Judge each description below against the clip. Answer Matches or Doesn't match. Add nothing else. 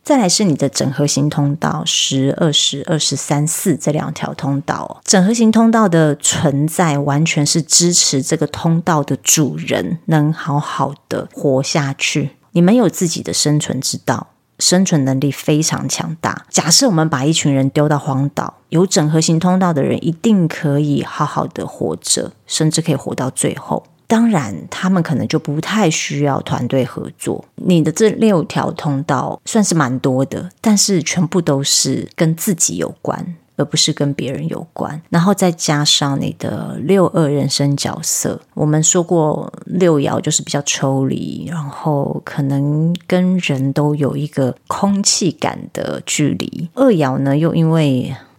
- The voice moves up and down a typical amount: Matches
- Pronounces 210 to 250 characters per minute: Matches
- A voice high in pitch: Doesn't match